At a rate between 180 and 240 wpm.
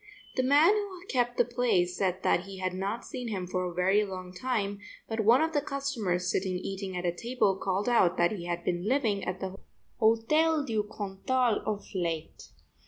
Yes: average, 195 wpm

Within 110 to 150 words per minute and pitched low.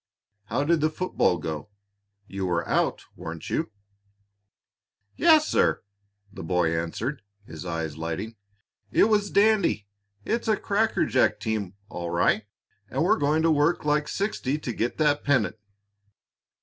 Yes: slow, 135 wpm; low, 130 Hz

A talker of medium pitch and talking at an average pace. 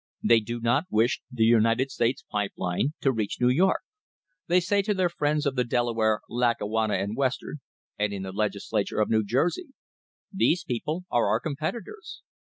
No: low, 120 Hz; average, 175 wpm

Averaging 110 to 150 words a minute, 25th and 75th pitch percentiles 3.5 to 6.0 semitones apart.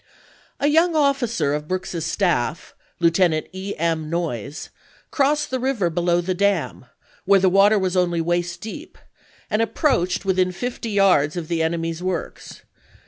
Yes: average, 145 wpm; average, 3.8 semitones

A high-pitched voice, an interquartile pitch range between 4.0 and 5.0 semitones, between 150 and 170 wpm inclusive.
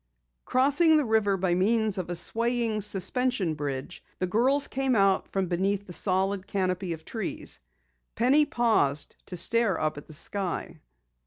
Yes: high, 200 Hz; average, 4.5 semitones; average, 155 wpm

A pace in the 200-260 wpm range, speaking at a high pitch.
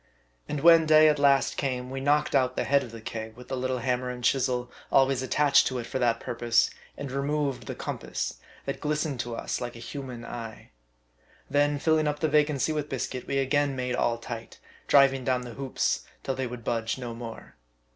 No: fast, 205 wpm; low, 130 Hz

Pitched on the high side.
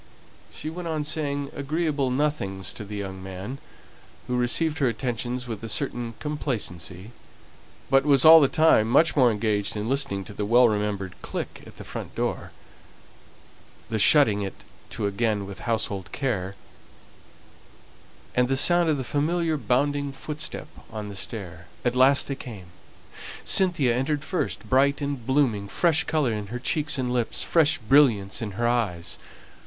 No: low, 125 Hz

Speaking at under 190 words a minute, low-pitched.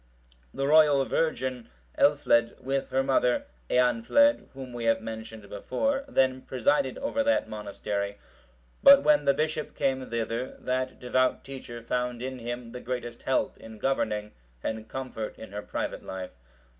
Yes: average, 145 wpm; low, 125 Hz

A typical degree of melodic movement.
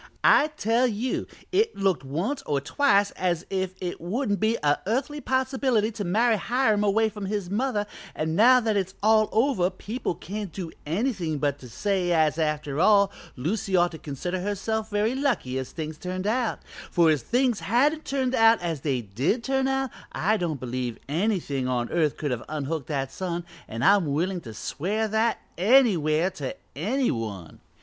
No: wide, 6.5 semitones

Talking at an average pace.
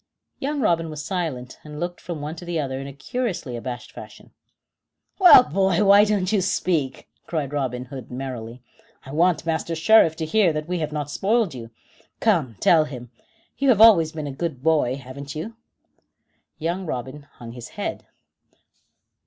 Yes: average, 170 wpm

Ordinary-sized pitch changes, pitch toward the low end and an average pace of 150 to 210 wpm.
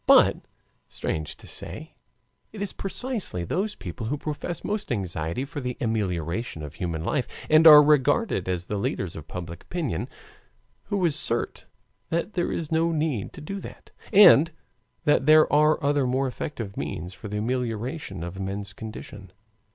No: wide, 8.8 semitones; low, 125 Hz; average, 160 wpm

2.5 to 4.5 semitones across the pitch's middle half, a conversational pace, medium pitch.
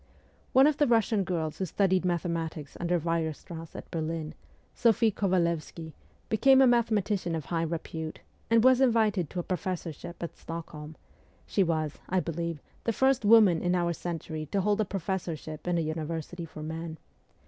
Yes: average, 4.1 semitones; average, 160 wpm; medium, 175 Hz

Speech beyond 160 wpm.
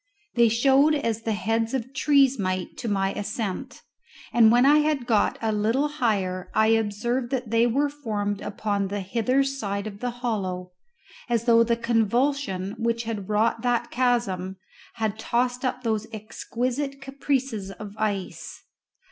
No: average, 155 wpm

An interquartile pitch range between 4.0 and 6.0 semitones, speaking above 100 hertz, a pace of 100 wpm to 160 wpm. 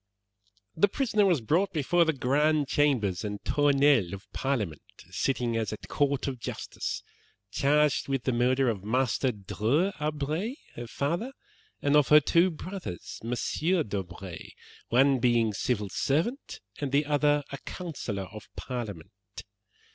Yes: average, 5.0 semitones; low, 135 Hz; average, 140 wpm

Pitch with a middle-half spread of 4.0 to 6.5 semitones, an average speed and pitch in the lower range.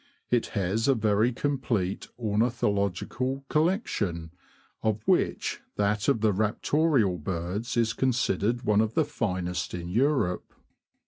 No: average, 4.7 semitones; slow, 120 wpm; low, 110 Hz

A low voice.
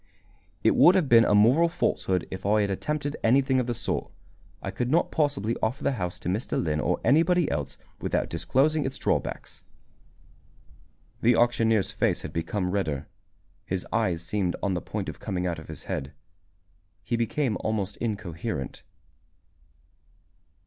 Yes: low, 110 Hz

